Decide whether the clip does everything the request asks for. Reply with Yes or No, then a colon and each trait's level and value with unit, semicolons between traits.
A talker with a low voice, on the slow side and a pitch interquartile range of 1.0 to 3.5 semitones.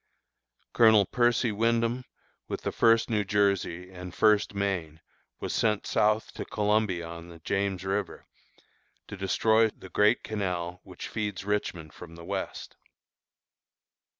Yes: low, 100 Hz; slow, 130 wpm; average, 3.2 semitones